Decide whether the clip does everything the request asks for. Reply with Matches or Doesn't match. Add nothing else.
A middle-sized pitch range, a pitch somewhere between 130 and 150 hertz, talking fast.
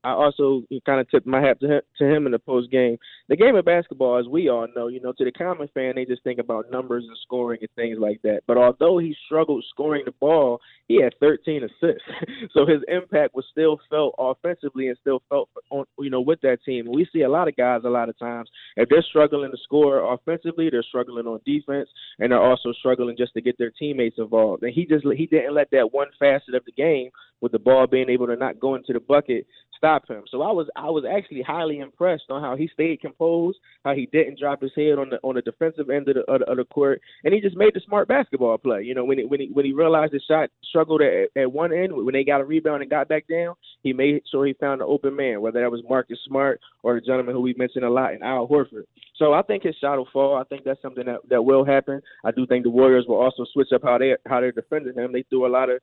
Matches